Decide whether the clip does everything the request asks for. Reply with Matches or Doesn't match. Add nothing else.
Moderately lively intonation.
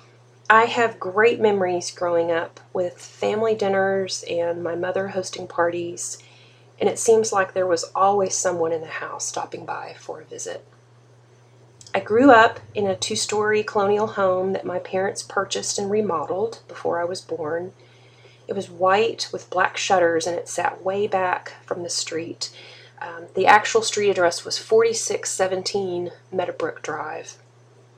Matches